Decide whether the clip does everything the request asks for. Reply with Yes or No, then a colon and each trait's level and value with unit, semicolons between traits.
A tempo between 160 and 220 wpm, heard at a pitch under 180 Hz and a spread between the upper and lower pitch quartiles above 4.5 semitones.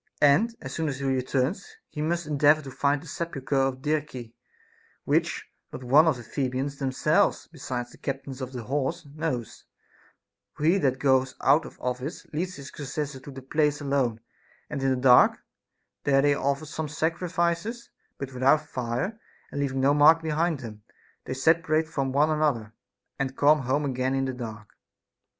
No: average, 175 wpm; medium, 140 Hz; average, 2.9 semitones